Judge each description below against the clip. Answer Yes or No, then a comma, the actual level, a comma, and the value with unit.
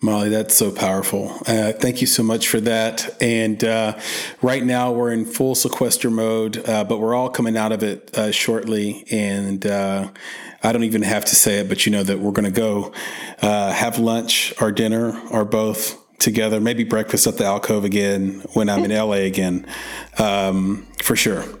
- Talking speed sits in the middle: Yes, average, 190 wpm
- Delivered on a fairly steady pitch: Yes, narrow, 1.9 semitones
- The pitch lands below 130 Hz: Yes, low, 110 Hz